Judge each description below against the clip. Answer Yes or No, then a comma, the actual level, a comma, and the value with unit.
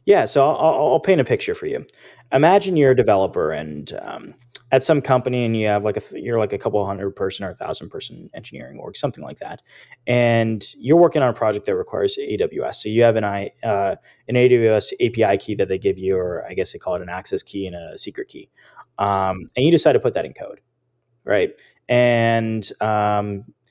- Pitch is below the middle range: Yes, low, 120 Hz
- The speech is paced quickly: Yes, fast, 220 wpm